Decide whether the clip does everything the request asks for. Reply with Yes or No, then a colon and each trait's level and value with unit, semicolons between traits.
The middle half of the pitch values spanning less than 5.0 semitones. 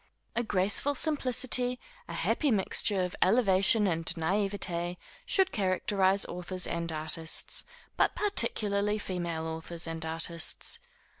Yes: average, 4.1 semitones